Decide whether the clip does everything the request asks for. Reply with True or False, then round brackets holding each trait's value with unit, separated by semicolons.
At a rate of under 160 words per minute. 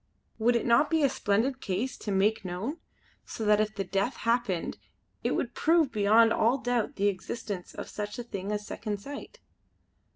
False (185 wpm)